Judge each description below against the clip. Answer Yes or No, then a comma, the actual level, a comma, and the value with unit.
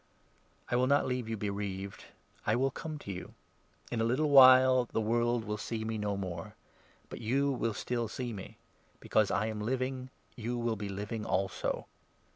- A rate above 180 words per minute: Yes, average, 190 wpm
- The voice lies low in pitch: Yes, low, 115 Hz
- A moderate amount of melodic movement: Yes, average, 3.4 semitones